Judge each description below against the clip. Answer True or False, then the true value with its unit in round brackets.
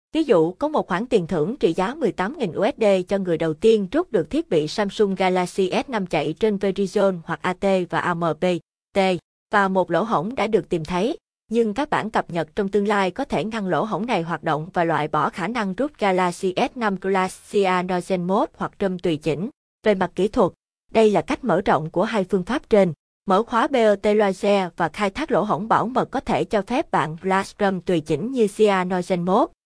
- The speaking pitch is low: False (195 Hz)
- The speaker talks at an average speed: True (210 wpm)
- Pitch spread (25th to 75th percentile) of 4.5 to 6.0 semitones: False (3.4 semitones)